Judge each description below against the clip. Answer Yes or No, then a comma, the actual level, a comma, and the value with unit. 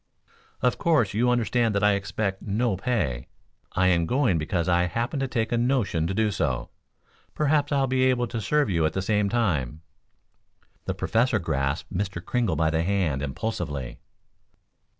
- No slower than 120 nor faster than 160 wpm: No, average, 170 wpm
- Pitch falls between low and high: No, low, 100 Hz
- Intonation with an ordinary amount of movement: No, wide, 6.6 semitones